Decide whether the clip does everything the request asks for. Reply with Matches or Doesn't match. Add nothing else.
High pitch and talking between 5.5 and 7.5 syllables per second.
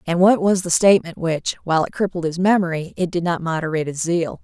Doesn't match